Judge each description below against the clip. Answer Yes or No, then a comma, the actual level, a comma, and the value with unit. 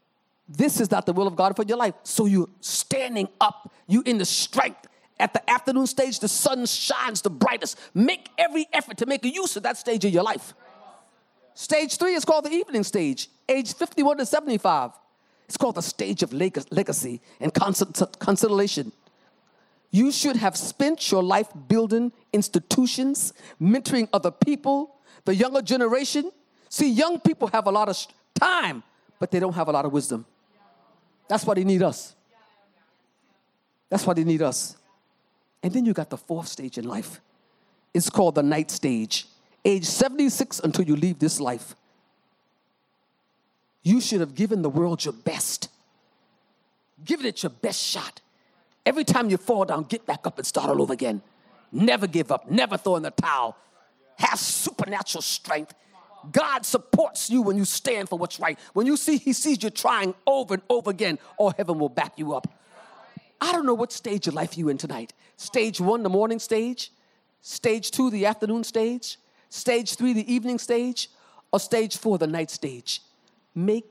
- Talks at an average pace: Yes, average, 175 wpm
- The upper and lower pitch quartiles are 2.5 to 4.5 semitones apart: No, average, 5.3 semitones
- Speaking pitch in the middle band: No, high, 220 Hz